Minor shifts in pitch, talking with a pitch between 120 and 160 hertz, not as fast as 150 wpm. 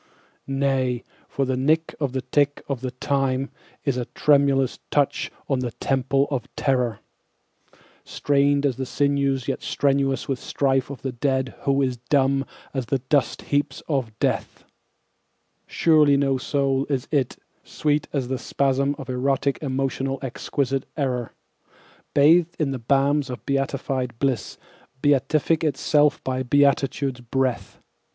Yes: narrow, 1.4 semitones; low, 135 Hz; average, 140 wpm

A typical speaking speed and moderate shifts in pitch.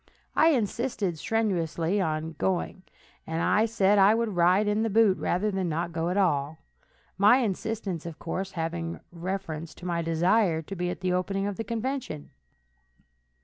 Yes: average, 160 wpm; average, 4.0 semitones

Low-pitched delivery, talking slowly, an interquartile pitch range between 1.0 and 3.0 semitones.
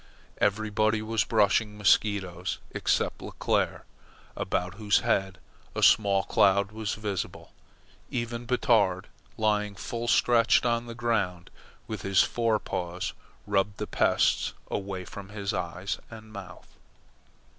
Yes: low, 105 Hz; slow, 115 wpm; narrow, 2.5 semitones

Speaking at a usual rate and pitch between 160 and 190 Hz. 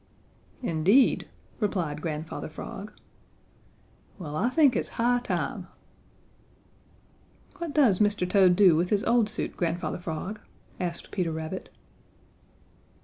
No: slow, 110 wpm; medium, 185 Hz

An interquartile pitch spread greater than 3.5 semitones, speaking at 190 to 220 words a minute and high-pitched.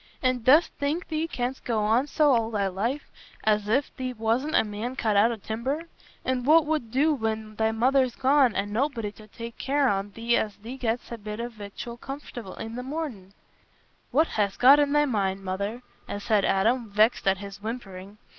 Yes: average, 4.0 semitones; average, 195 wpm; high, 230 Hz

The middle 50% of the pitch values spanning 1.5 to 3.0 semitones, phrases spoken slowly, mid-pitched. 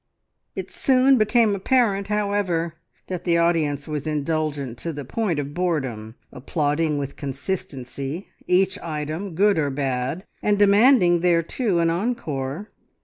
No: wide, 5.6 semitones; slow, 130 wpm; medium, 165 Hz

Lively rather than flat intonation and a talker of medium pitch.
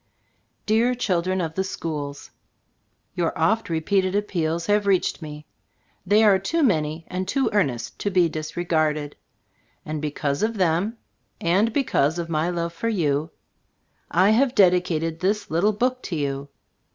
No: average, 4.6 semitones; medium, 175 Hz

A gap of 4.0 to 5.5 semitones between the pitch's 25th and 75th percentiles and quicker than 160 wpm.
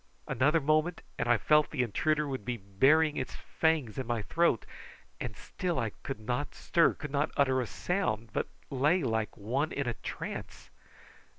Yes: average, 4.6 semitones; average, 175 wpm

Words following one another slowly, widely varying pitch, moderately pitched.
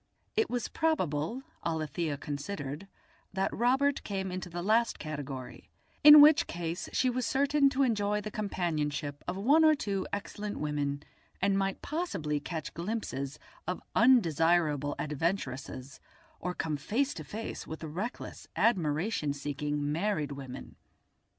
Yes: slow, 130 wpm; wide, 7.4 semitones; medium, 180 Hz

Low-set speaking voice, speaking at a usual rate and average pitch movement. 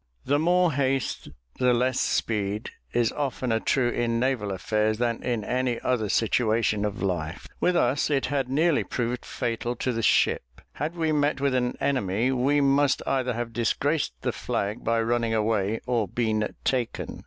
Yes: low, 120 Hz; average, 165 wpm; average, 3.4 semitones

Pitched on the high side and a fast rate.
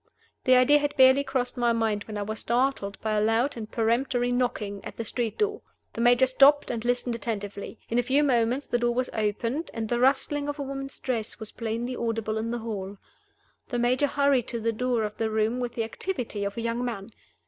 Yes: high, 240 Hz; fast, 220 wpm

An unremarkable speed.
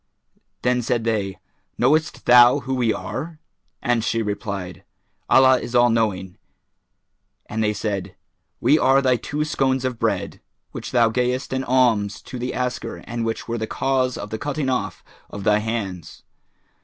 Yes: average, 160 wpm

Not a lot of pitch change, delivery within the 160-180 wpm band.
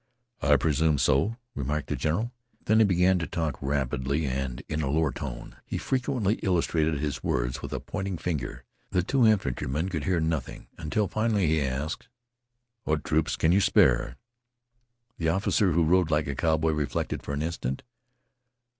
No: average, 4.6 semitones; average, 165 wpm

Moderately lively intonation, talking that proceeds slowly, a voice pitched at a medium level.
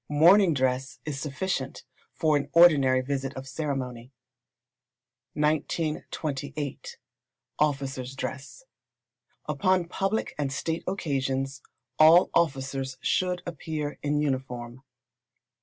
Yes: average, 3.2 semitones; slow, 90 wpm; medium, 145 Hz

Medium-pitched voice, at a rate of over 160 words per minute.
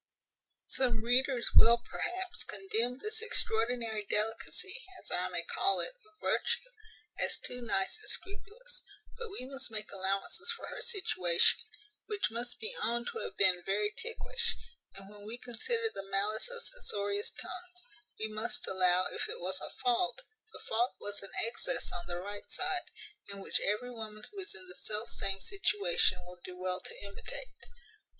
No: high, 235 Hz; average, 170 wpm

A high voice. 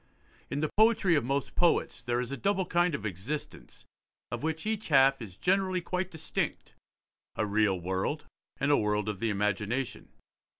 No: medium, 140 Hz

